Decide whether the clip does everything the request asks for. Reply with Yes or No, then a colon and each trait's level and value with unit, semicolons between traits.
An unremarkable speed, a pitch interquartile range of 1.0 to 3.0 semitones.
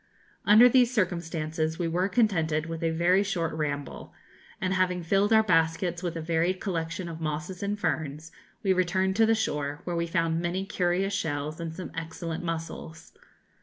Yes: average, 170 wpm; narrow, 2.6 semitones